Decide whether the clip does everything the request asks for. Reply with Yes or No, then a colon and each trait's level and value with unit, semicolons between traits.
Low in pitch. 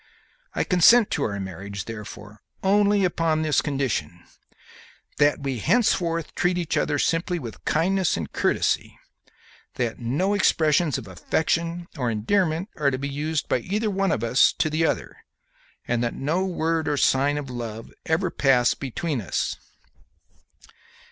No: medium, 150 Hz